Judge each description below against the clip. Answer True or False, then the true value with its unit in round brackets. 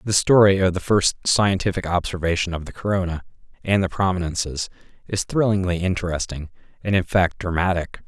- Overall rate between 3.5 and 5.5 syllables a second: False (5.7 syllables/s)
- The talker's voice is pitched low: True (90 Hz)